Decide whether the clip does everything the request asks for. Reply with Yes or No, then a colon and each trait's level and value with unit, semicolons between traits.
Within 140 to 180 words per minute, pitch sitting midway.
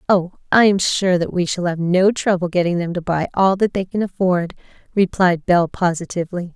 No: average, 200 wpm; medium, 180 Hz